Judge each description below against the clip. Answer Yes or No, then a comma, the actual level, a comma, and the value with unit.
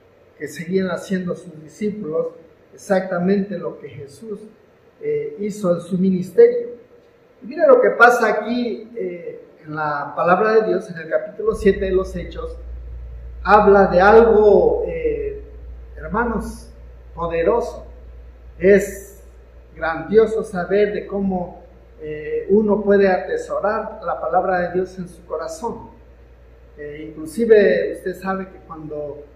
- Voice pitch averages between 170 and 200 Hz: Yes, high, 190 Hz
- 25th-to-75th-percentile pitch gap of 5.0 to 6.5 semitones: Yes, wide, 5.5 semitones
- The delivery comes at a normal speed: No, slow, 125 wpm